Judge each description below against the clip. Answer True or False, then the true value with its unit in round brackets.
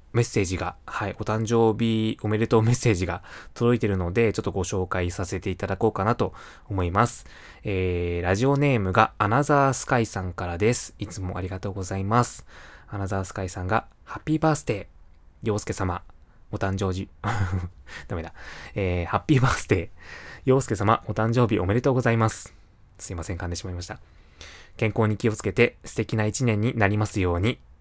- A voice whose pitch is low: True (105 Hz)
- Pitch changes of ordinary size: True (3.7 semitones)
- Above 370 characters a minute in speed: True (385 characters per minute)